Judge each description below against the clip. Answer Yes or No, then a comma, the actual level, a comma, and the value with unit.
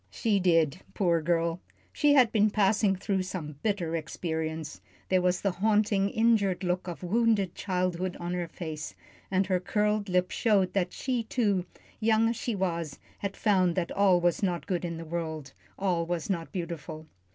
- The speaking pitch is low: No, medium, 185 Hz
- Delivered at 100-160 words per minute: No, average, 175 wpm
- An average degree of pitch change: Yes, average, 3.2 semitones